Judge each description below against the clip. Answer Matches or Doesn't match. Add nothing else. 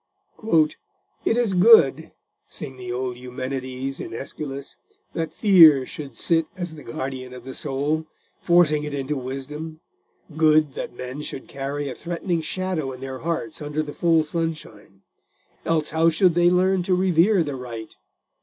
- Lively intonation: Doesn't match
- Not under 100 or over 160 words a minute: Matches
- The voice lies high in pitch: Doesn't match